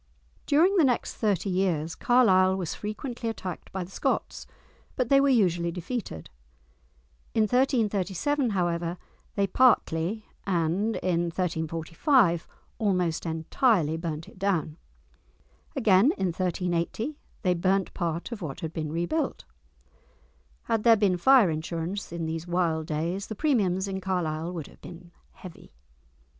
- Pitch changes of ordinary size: Yes, average, 4.6 semitones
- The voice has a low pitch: No, medium, 185 Hz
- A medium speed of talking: No, slow, 130 wpm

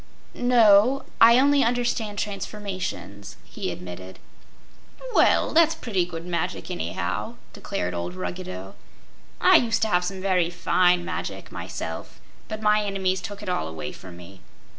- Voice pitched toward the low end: No, medium, 185 Hz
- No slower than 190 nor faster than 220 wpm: No, average, 140 wpm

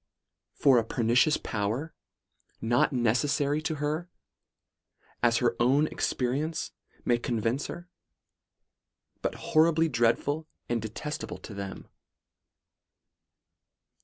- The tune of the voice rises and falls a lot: No, average, 4.6 semitones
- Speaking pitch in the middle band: No, low, 125 Hz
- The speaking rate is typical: No, slow, 100 wpm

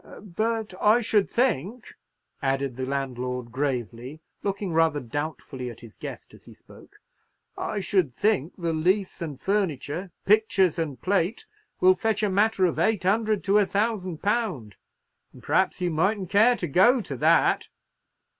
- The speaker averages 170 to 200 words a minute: No, average, 155 wpm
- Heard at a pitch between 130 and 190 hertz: Yes, medium, 185 Hz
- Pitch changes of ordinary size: No, wide, 6.8 semitones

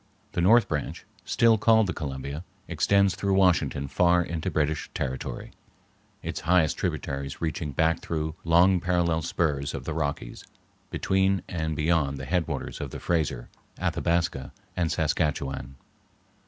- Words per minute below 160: Yes, slow, 135 wpm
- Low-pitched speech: Yes, very low, 80 Hz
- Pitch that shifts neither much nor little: Yes, average, 3.8 semitones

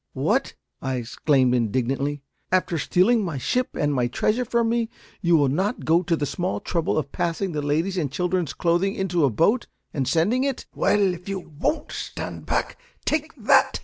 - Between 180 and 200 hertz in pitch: No, medium, 170 Hz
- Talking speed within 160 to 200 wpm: Yes, average, 185 wpm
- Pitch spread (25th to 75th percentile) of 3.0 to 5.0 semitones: No, wide, 5.5 semitones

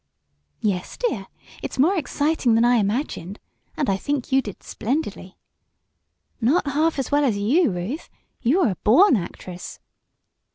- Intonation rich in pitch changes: Yes, wide, 6.6 semitones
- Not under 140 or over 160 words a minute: Yes, average, 150 wpm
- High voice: Yes, very high, 250 Hz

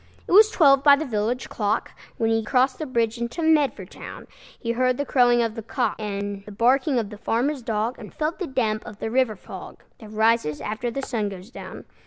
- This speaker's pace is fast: Yes, fast, 220 wpm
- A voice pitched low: No, high, 235 Hz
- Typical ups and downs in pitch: Yes, average, 3.5 semitones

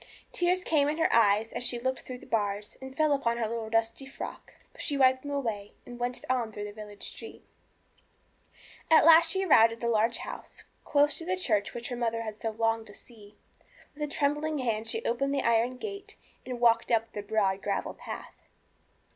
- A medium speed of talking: No, fast, 210 wpm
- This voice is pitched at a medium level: No, high, 240 Hz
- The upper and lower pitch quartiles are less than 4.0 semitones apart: No, average, 4.5 semitones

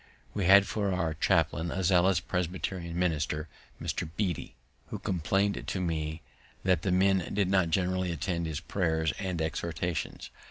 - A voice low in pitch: Yes, very low, 90 Hz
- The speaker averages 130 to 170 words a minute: Yes, average, 150 wpm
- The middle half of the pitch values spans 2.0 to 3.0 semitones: Yes, average, 2.7 semitones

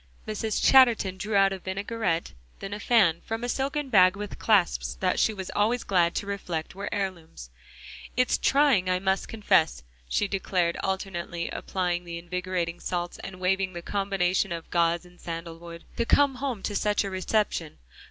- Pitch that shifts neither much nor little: Yes, average, 3.1 semitones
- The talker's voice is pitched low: No, high, 190 Hz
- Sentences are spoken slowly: No, average, 170 wpm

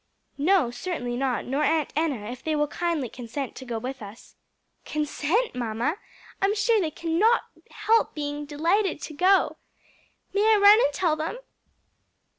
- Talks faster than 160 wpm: No, average, 155 wpm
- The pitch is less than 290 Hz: No, very high, 305 Hz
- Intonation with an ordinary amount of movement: No, wide, 6.5 semitones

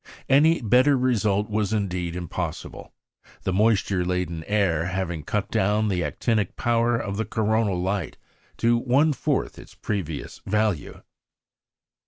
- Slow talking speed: Yes, slow, 130 wpm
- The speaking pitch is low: Yes, low, 105 Hz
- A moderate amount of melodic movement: Yes, average, 4.0 semitones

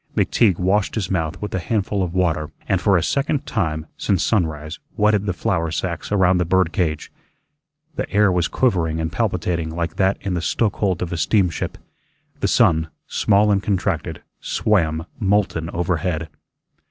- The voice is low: Yes, very low, 90 Hz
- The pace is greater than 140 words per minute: Yes, average, 165 wpm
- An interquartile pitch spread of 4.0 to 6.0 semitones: No, average, 3.6 semitones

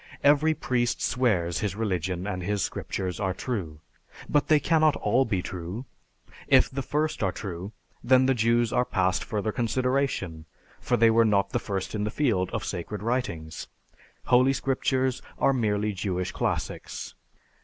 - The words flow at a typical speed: Yes, average, 155 wpm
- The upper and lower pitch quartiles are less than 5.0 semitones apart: No, wide, 5.5 semitones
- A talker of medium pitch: No, low, 110 Hz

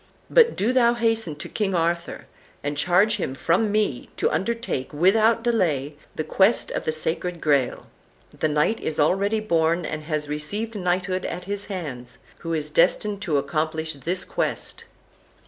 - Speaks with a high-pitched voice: No, medium, 175 Hz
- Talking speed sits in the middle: Yes, average, 160 wpm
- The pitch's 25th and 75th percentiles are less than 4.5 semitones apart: No, wide, 5.4 semitones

